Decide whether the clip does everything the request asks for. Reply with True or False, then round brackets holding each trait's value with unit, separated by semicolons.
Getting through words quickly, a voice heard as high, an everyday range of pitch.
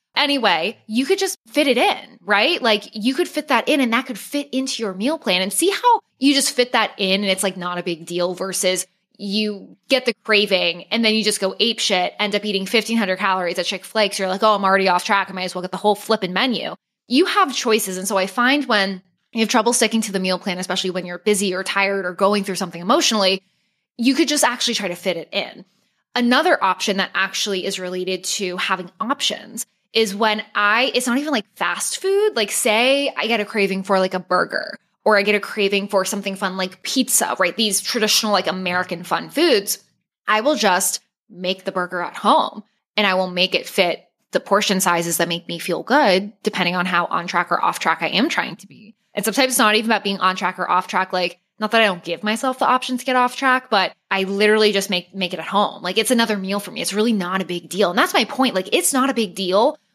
True (245 wpm; 205 Hz; 4.1 semitones)